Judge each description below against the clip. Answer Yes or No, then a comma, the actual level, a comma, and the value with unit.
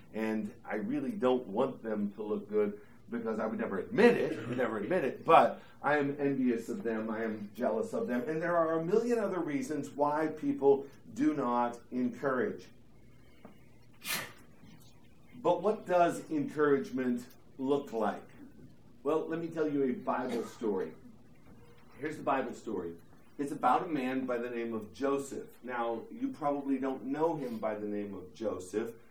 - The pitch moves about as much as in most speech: No, wide, 5.8 semitones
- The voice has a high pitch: No, low, 135 Hz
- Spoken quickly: No, average, 165 wpm